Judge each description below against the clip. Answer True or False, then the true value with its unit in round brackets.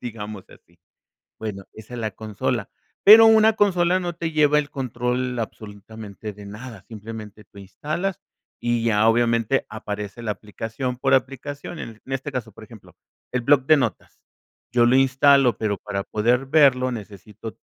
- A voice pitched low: True (120 Hz)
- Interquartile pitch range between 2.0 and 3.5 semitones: False (4.2 semitones)